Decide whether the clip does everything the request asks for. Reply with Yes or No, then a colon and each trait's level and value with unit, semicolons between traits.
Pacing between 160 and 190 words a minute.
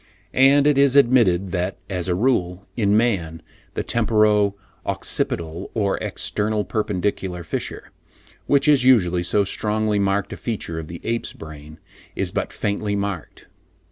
No: average, 140 wpm